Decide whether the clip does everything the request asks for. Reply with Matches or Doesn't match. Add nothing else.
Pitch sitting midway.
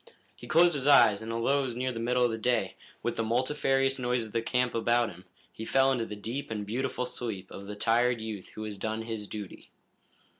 Doesn't match